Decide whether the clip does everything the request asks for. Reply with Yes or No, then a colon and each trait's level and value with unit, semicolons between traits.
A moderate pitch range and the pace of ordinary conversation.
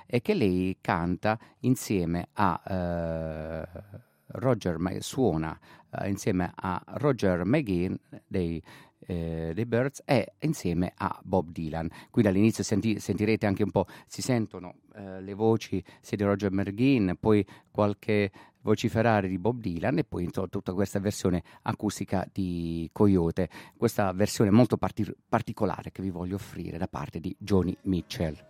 Yes: average, 3.4 semitones; average, 145 wpm